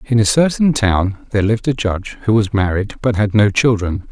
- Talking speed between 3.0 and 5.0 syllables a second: No, 5.4 syllables/s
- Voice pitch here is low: Yes, low, 110 Hz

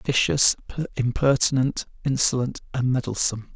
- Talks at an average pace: No, slow, 85 wpm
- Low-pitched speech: Yes, low, 130 Hz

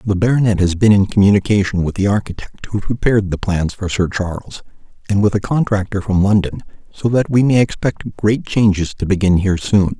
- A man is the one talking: Yes, male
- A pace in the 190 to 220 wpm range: Yes, average, 200 wpm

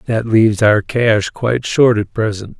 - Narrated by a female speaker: No, male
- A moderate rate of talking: Yes, average, 185 wpm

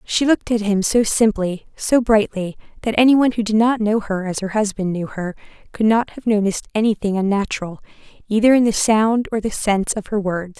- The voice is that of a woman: Yes, female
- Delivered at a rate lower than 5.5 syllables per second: No, 5.6 syllables/s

